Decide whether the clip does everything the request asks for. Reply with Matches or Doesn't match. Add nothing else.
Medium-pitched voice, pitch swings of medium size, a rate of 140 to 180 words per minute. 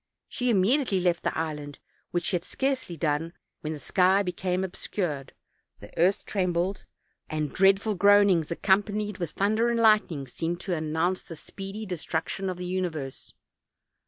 Matches